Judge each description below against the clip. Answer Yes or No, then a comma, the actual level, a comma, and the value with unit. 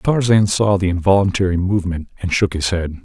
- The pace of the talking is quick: No, average, 180 wpm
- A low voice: Yes, very low, 95 Hz